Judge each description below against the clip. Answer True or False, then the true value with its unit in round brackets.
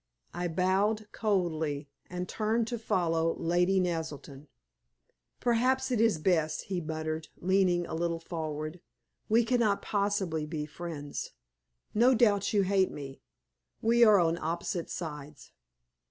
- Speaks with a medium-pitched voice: True (175 Hz)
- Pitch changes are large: False (4.6 semitones)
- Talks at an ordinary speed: False (125 wpm)